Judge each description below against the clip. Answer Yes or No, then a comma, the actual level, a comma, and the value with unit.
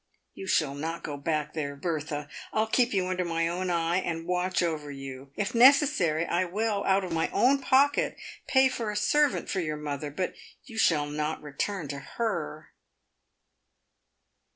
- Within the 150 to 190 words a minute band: Yes, average, 170 wpm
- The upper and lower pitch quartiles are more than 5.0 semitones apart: Yes, wide, 5.4 semitones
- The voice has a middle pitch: Yes, medium, 170 Hz